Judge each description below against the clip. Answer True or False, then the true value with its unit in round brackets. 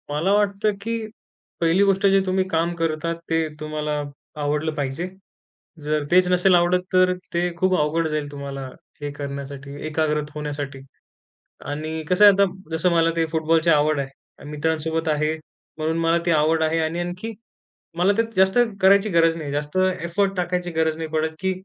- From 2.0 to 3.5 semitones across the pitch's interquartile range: True (3.1 semitones)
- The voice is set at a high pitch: False (160 Hz)